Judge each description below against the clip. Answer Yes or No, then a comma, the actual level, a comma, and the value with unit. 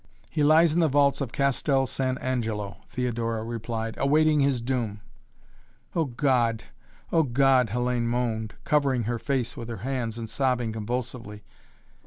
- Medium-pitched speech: No, low, 125 Hz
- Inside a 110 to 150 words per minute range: Yes, average, 145 wpm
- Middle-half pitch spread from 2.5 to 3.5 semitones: Yes, average, 3.2 semitones